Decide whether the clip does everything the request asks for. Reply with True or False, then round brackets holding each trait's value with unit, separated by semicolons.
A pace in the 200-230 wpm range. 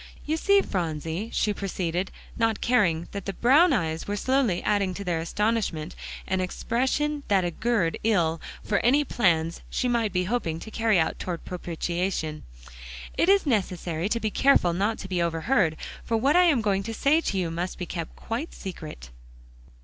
False (175 wpm)